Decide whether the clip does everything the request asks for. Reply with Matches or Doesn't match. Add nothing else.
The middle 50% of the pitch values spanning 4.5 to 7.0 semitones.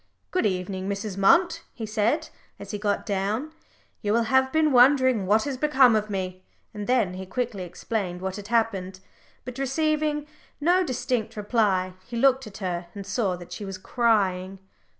Matches